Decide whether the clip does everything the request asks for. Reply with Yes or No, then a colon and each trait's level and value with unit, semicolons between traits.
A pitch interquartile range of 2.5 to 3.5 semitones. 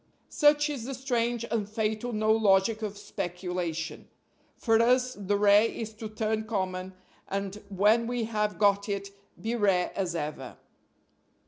Yes: average, 2.8 semitones